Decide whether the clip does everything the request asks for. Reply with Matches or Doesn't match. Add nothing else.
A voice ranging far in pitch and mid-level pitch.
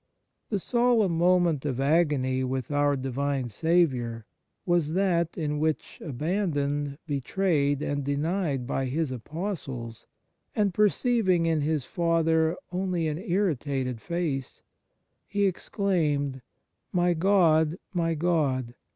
Doesn't match